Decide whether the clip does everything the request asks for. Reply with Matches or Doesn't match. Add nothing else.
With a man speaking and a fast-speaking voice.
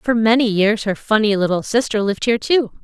Doesn't match